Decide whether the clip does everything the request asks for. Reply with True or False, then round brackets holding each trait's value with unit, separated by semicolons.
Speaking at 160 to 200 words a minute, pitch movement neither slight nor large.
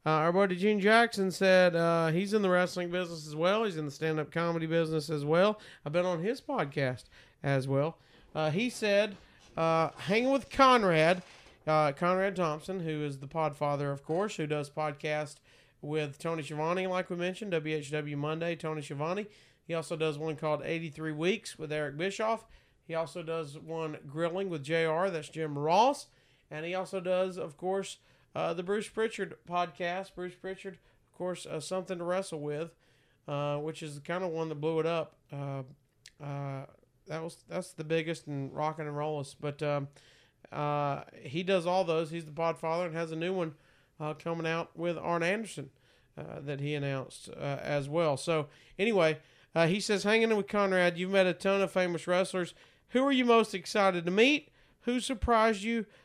True (190 wpm; 3.8 semitones)